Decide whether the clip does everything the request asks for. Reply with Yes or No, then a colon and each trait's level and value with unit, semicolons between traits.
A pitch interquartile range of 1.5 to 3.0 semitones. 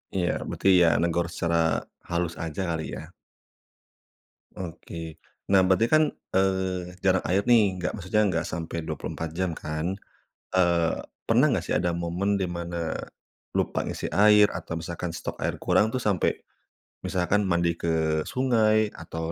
Yes: average, 2.7 semitones